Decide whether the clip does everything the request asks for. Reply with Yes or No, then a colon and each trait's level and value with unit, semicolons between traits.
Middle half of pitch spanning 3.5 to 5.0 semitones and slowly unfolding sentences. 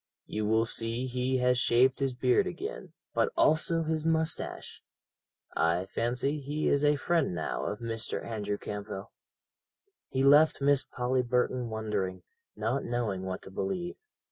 No: average, 4.7 semitones; average, 145 wpm